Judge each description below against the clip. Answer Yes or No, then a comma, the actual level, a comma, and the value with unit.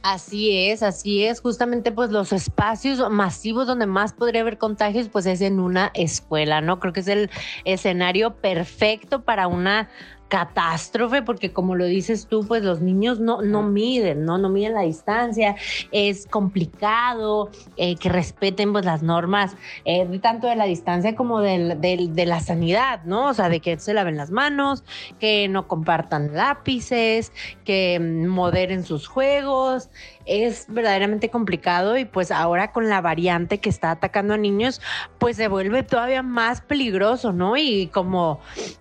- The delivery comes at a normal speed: Yes, average, 160 wpm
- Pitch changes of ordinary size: Yes, average, 4.0 semitones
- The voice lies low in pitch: No, high, 205 Hz